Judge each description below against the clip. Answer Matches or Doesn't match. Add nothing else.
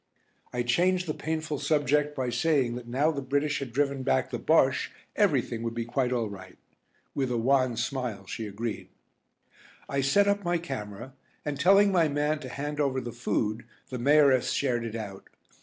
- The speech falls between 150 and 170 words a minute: Doesn't match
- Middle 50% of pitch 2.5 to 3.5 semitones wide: Doesn't match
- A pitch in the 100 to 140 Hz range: Matches